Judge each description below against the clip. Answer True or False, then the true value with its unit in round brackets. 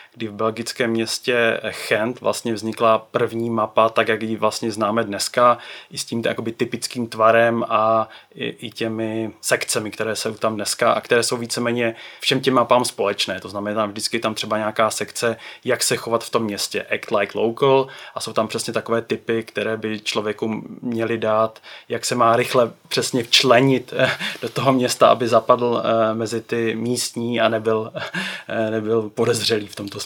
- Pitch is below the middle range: True (115 Hz)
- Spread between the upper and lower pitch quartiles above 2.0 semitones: False (1.1 semitones)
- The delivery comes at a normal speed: False (175 wpm)